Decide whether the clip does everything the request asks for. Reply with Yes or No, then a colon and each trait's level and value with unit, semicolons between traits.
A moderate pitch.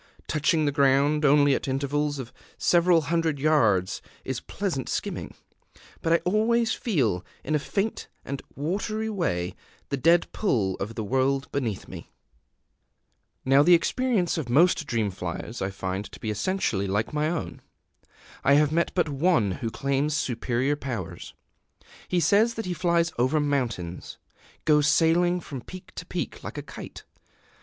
Yes: medium, 145 Hz